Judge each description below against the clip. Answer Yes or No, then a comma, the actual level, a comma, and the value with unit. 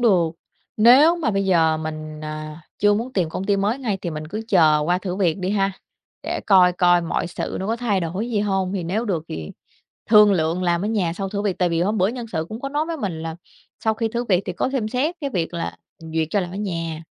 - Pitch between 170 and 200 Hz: Yes, high, 190 Hz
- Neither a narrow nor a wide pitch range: Yes, average, 4.4 semitones